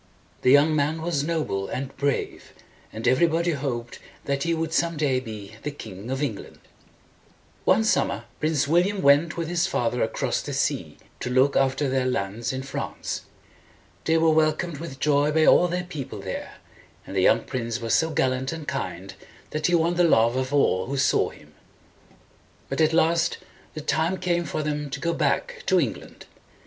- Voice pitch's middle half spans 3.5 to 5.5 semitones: Yes, average, 4.0 semitones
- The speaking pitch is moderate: Yes, medium, 145 Hz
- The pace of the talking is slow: No, average, 185 wpm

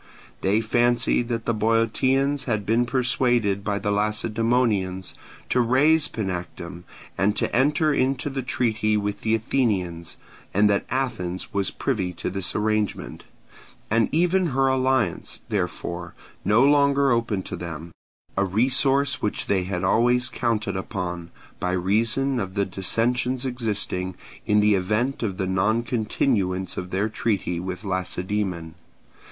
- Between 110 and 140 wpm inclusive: Yes, slow, 135 wpm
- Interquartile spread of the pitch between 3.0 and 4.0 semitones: No, average, 4.8 semitones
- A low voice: Yes, low, 110 Hz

